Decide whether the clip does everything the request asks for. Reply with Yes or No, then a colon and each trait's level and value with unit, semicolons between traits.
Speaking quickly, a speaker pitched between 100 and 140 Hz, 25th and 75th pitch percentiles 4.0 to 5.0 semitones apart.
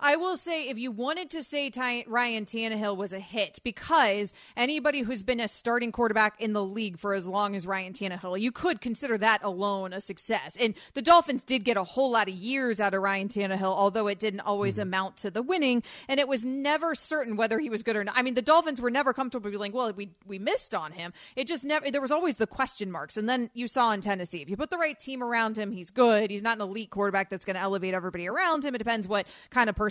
No: fast, 255 wpm; high, 225 Hz; average, 4.6 semitones